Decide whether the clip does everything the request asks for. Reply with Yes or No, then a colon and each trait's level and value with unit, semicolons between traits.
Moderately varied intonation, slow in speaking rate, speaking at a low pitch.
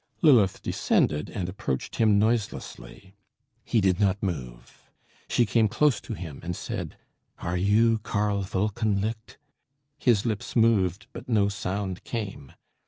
Yes: average, 3.2 semitones; slow, 130 wpm; low, 100 Hz